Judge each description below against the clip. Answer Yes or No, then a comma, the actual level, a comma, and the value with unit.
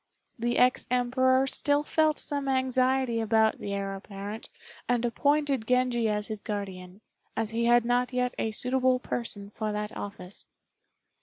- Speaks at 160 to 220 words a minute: No, average, 150 wpm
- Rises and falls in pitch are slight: No, average, 3.4 semitones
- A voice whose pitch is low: No, high, 240 Hz